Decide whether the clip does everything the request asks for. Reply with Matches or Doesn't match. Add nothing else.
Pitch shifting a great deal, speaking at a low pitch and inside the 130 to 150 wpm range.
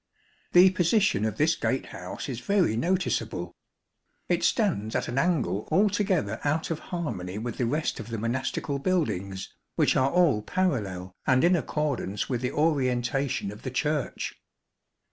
Matches